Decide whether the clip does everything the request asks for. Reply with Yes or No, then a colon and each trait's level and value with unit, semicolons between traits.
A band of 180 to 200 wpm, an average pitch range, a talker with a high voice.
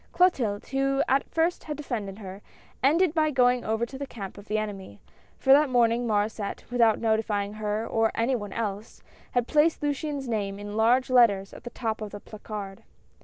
Yes: average, 185 wpm; average, 4.5 semitones; high, 230 Hz